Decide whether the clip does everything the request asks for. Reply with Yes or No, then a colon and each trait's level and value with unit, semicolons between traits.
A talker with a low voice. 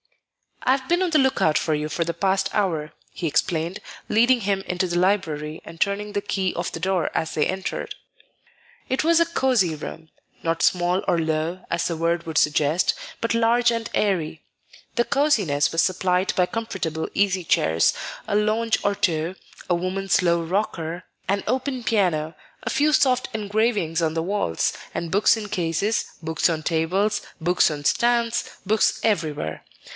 No: medium, 185 Hz